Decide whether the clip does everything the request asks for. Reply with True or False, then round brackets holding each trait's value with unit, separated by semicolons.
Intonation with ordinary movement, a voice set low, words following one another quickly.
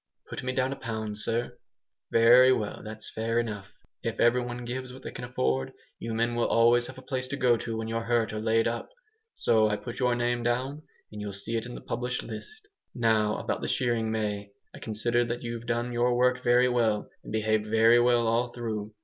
False (1.8 semitones; 120 Hz; 220 wpm)